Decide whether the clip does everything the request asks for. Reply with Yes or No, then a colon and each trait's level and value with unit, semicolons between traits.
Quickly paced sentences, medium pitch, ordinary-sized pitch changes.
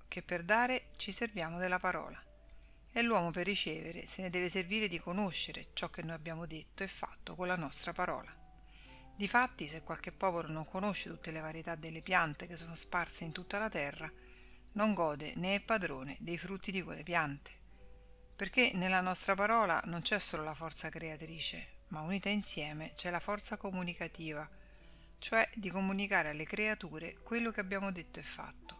Yes: fast, 175 wpm; medium, 175 Hz; average, 3.6 semitones